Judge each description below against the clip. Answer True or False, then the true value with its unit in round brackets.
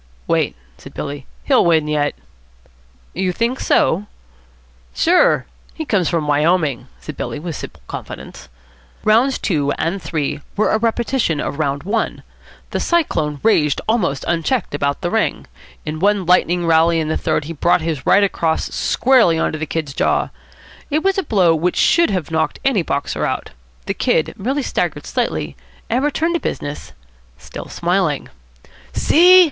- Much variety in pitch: True (6.7 semitones)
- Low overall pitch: False (170 Hz)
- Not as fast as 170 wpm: True (160 wpm)